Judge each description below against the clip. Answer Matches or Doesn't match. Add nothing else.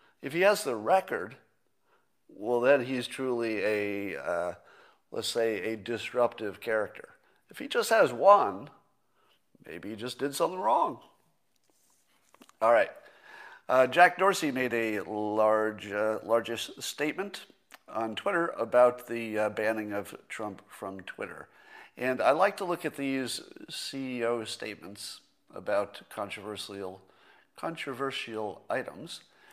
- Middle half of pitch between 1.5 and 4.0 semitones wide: Doesn't match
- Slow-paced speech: Matches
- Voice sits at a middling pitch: Doesn't match